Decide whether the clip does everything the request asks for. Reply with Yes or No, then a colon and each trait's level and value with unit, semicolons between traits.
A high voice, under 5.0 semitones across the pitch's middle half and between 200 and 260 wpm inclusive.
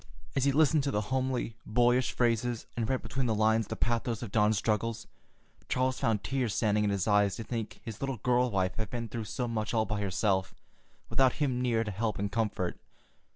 No: low, 115 Hz; average, 2.8 semitones; fast, 205 wpm